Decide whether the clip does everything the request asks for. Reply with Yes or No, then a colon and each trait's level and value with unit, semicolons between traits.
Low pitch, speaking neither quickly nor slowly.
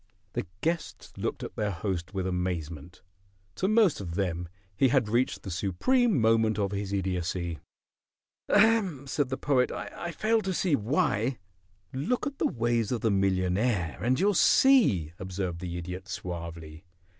Yes: low, 105 Hz; average, 155 wpm